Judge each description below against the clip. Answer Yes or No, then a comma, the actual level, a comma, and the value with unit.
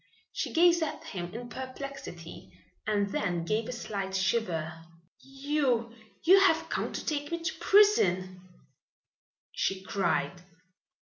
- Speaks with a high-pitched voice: Yes, high, 235 Hz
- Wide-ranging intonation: Yes, wide, 8.0 semitones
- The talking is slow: Yes, slow, 125 wpm